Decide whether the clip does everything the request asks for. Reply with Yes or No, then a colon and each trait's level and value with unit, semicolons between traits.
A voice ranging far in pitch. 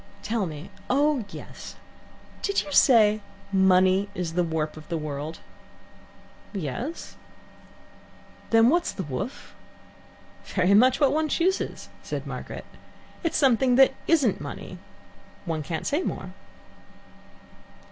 Yes: wide, 8.3 semitones